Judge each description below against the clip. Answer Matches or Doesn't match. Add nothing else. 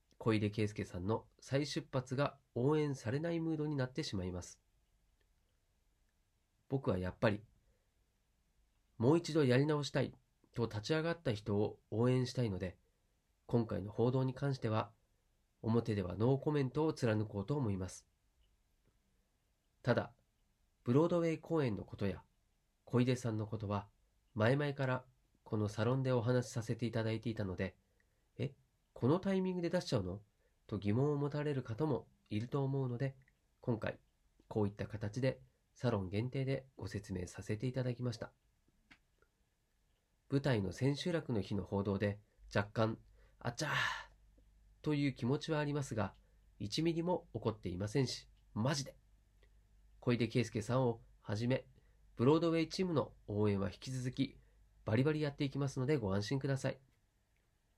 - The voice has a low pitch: Matches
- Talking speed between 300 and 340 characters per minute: Matches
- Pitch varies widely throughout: Doesn't match